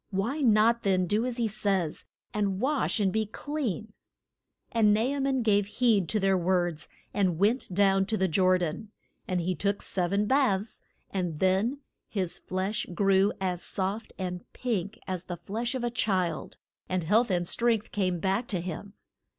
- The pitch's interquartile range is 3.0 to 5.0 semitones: Yes, average, 3.3 semitones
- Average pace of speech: Yes, average, 175 wpm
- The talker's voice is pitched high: Yes, high, 200 Hz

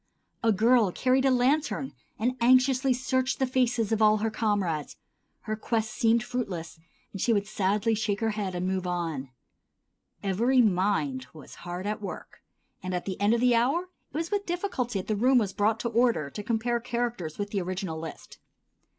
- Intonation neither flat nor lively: Yes, average, 4.5 semitones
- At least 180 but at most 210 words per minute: Yes, average, 185 wpm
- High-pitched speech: Yes, high, 220 Hz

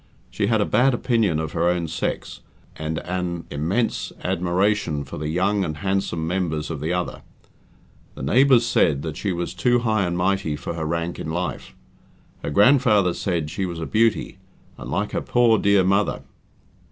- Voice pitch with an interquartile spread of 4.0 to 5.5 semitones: Yes, average, 4.3 semitones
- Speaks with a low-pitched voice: Yes, very low, 90 Hz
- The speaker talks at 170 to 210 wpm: Yes, average, 175 wpm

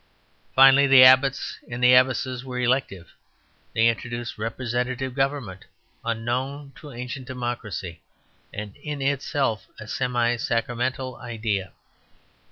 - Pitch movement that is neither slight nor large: No, narrow, 2.3 semitones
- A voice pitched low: Yes, low, 125 Hz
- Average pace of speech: No, slow, 105 wpm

